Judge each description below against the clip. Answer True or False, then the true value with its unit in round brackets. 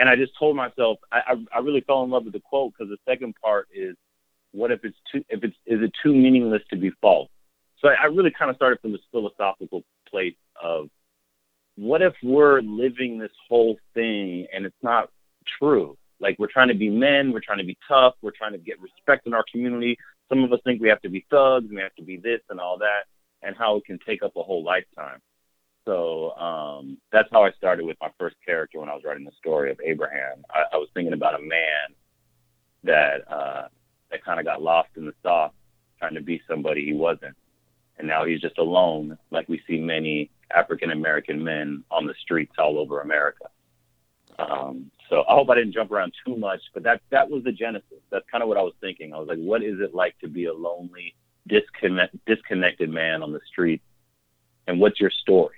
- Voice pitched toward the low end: True (105 Hz)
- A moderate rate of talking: False (220 wpm)